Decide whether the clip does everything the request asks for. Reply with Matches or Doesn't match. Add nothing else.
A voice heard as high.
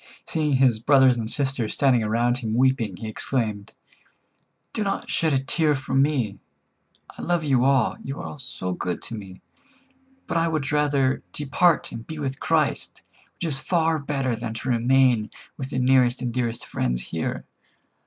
Doesn't match